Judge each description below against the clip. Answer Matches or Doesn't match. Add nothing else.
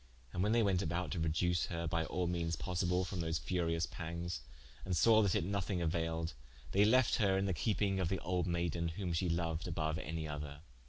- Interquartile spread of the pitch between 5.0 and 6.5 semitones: Doesn't match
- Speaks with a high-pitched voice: Doesn't match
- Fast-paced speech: Matches